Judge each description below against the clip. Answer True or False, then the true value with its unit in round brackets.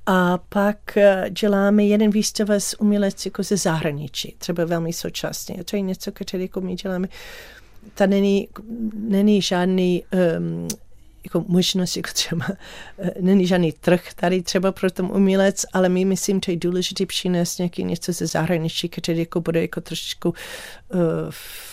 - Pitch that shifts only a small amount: True (2.3 semitones)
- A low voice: False (185 Hz)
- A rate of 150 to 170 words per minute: True (155 wpm)